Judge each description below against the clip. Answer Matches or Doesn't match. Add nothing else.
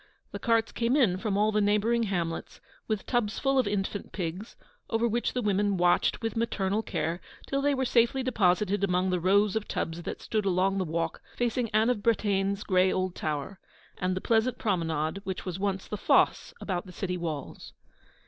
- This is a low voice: Doesn't match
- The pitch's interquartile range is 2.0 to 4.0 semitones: Matches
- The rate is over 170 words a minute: Matches